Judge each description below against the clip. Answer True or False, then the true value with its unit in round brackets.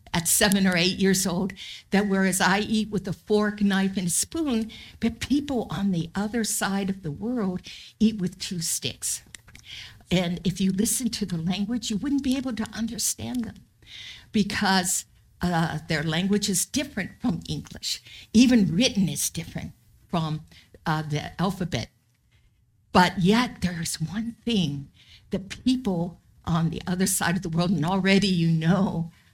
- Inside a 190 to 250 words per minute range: False (160 wpm)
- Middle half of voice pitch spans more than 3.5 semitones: True (4.1 semitones)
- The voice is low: False (190 Hz)